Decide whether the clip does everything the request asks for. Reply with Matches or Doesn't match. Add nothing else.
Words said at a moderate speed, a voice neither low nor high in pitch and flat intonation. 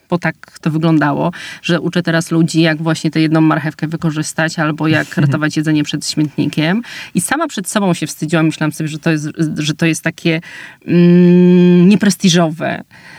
Doesn't match